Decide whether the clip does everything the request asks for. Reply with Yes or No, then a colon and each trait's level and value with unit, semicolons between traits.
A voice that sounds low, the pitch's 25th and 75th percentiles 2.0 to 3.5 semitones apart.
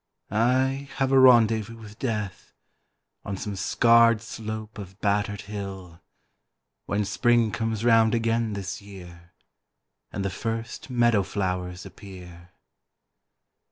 Yes: low, 105 Hz; average, 2.9 semitones